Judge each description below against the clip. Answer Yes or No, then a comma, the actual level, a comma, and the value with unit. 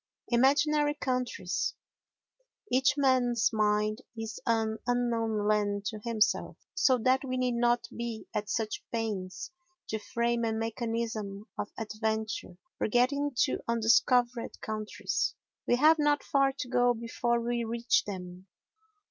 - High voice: Yes, high, 235 Hz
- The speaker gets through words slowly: Yes, slow, 130 wpm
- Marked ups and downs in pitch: No, narrow, 2.5 semitones